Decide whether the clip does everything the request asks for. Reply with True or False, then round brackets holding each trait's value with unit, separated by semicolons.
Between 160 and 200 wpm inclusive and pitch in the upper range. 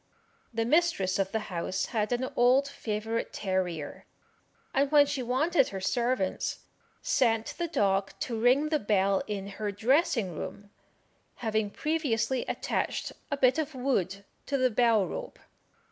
False (145 wpm; 230 Hz)